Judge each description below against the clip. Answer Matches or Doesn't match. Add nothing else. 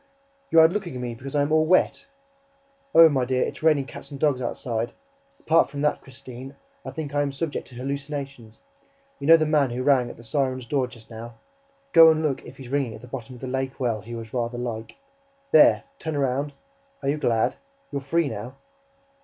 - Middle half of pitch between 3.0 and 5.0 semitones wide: Matches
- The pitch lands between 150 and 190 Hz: Doesn't match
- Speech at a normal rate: Doesn't match